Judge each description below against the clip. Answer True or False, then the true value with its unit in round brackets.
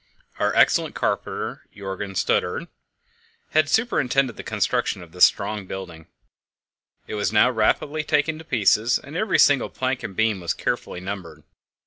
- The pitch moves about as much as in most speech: False (6.6 semitones)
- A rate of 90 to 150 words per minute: True (145 wpm)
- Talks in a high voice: False (110 Hz)